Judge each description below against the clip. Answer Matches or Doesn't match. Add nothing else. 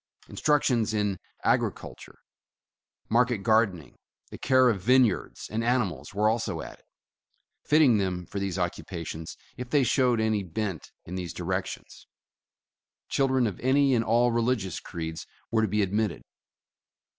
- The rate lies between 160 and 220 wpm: Doesn't match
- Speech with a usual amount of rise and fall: Matches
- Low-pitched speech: Matches